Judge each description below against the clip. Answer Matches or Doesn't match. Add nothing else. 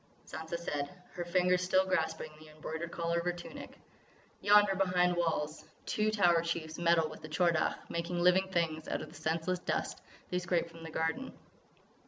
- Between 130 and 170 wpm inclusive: Doesn't match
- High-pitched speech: Doesn't match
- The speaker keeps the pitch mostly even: Matches